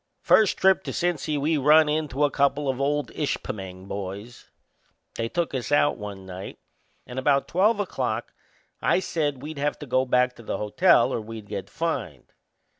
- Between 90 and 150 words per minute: No, average, 175 wpm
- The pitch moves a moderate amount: No, wide, 5.8 semitones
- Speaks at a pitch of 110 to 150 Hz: Yes, medium, 140 Hz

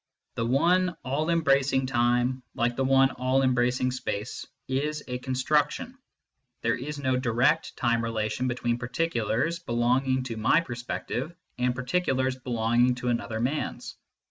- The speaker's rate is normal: Yes, average, 145 wpm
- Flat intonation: Yes, narrow, 2.2 semitones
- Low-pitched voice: Yes, low, 130 Hz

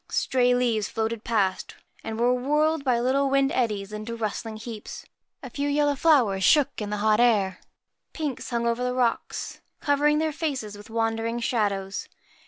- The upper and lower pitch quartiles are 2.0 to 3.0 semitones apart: No, average, 4.2 semitones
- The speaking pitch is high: Yes, high, 235 Hz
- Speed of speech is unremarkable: Yes, average, 165 wpm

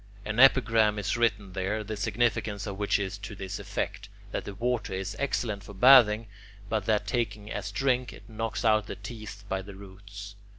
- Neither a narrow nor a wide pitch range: No, narrow, 2.1 semitones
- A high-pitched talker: No, low, 105 Hz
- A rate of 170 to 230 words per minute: Yes, average, 185 wpm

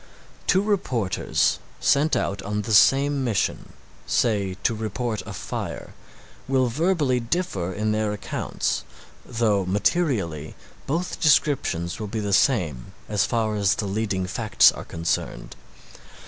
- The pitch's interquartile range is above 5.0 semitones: Yes, wide, 5.4 semitones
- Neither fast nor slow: No, slow, 130 wpm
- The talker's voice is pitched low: Yes, low, 110 Hz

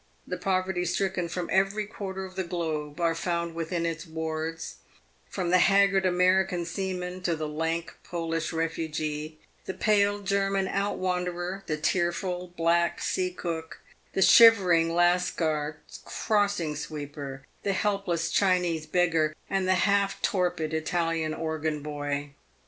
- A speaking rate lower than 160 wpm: Yes, average, 140 wpm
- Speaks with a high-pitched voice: No, medium, 175 Hz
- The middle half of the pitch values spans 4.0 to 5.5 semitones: No, average, 2.7 semitones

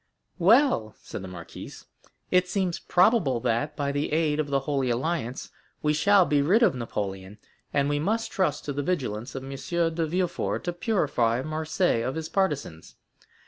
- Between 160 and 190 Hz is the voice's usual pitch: No, medium, 150 Hz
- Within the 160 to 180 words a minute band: Yes, average, 170 wpm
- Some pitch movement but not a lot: No, wide, 5.7 semitones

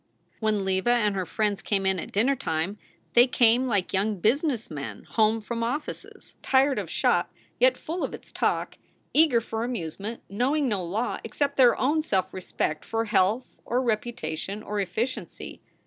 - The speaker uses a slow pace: No, average, 165 wpm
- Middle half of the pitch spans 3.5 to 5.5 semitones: Yes, average, 4.3 semitones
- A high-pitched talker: Yes, high, 220 Hz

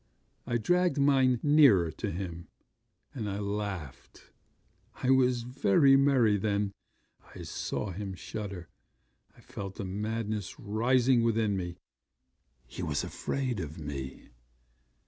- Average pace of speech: No, slow, 120 wpm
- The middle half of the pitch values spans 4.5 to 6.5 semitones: Yes, average, 4.9 semitones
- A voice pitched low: Yes, low, 105 Hz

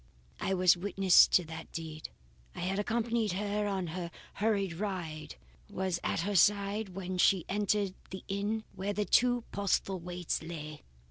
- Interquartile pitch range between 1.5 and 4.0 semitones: Yes, average, 2.7 semitones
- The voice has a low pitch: No, high, 190 Hz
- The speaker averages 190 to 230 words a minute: No, average, 155 wpm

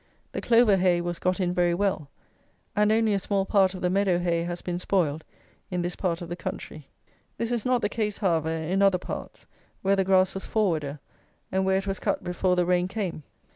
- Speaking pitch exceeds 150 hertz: Yes, medium, 185 Hz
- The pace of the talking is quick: Yes, fast, 215 wpm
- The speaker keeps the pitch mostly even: Yes, narrow, 2.3 semitones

